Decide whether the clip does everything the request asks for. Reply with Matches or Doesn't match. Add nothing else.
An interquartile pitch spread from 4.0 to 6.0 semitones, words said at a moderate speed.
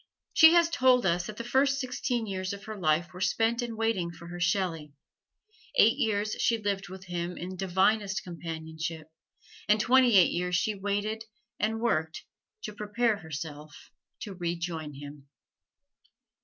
Matches